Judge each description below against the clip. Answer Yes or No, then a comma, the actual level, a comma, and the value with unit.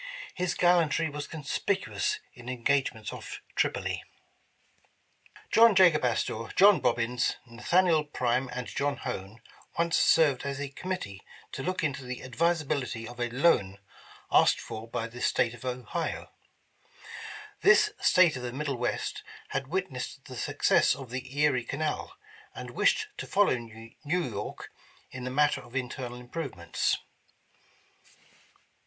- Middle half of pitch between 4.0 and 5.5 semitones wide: Yes, average, 4.7 semitones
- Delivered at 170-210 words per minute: No, slow, 135 wpm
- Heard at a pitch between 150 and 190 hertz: No, low, 135 Hz